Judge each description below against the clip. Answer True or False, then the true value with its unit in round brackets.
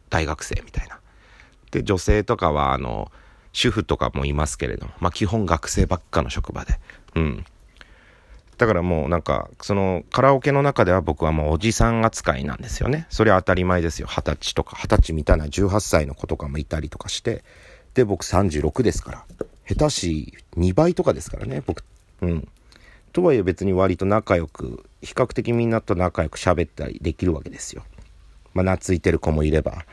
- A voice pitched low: True (90 Hz)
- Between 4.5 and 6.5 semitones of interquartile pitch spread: True (5.2 semitones)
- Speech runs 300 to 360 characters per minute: True (350 characters per minute)